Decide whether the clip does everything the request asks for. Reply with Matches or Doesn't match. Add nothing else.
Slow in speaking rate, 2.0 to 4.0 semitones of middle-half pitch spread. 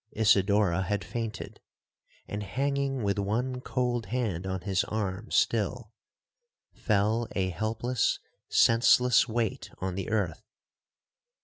Matches